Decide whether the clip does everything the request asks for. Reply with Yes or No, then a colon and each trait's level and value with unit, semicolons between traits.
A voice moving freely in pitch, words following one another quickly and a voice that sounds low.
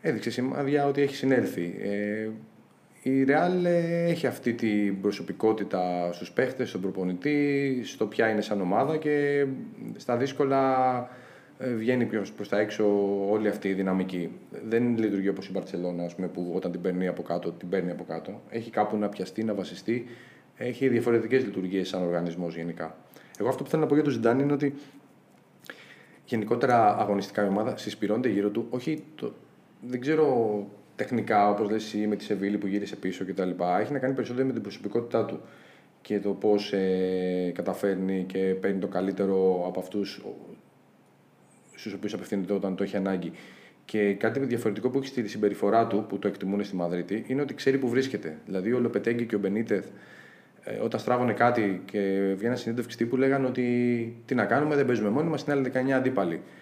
No: average, 4.6 semitones; fast, 175 wpm; low, 105 Hz